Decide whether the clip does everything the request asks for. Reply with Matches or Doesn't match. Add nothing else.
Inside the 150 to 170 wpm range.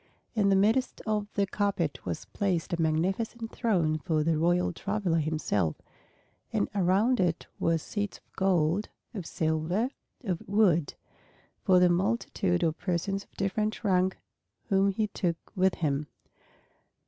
Doesn't match